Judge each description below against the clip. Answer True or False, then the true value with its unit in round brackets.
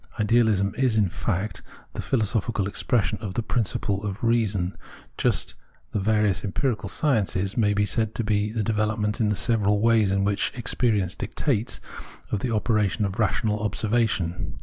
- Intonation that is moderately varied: False (2.3 semitones)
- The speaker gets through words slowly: False (155 wpm)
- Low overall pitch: True (105 Hz)